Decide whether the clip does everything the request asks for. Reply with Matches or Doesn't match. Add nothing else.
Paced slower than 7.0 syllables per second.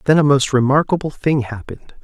Matches